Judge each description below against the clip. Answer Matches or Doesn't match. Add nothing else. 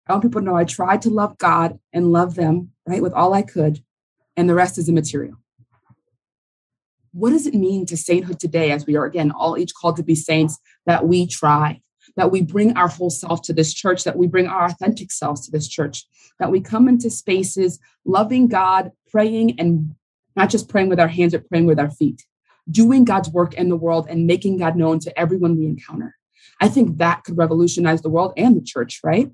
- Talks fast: Matches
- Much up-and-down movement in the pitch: Doesn't match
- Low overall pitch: Doesn't match